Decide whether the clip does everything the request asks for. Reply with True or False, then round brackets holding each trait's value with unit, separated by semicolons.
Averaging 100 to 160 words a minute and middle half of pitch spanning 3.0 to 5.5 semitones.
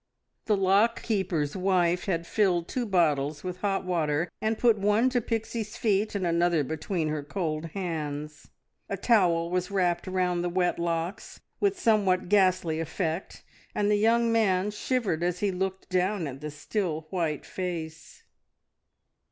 True (150 wpm; 3.7 semitones)